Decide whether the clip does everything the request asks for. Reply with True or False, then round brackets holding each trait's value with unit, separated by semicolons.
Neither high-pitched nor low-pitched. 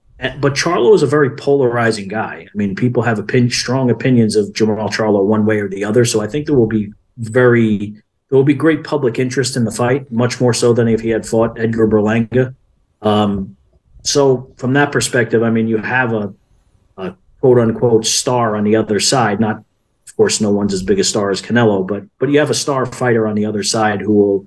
False (115 Hz)